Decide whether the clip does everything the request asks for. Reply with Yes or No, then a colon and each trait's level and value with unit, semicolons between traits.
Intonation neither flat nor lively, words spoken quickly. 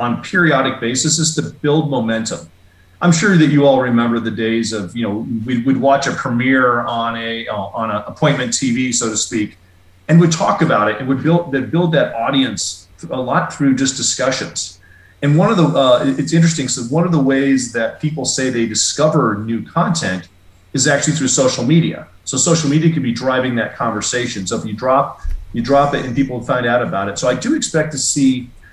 Yes: average, 4.3 semitones; fast, 210 wpm